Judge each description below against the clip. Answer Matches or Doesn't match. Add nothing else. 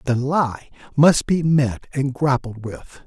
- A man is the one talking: Matches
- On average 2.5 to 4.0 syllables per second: Matches